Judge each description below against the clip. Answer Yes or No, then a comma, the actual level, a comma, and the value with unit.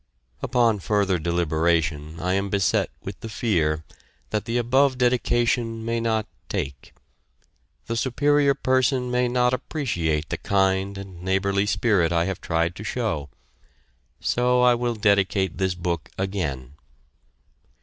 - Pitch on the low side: Yes, low, 100 Hz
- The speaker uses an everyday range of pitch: No, wide, 5.8 semitones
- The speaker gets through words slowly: Yes, slow, 130 wpm